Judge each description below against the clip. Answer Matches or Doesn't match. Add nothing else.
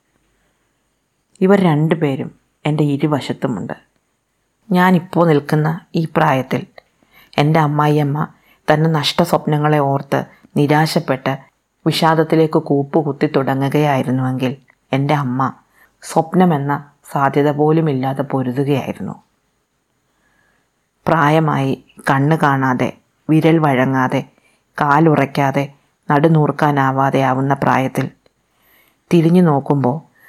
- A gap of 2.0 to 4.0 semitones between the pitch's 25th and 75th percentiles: Matches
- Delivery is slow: Doesn't match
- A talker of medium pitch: Matches